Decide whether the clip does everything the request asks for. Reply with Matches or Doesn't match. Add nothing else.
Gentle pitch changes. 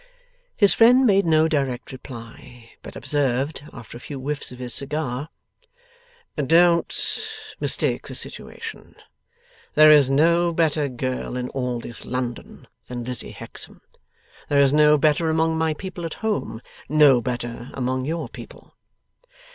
Doesn't match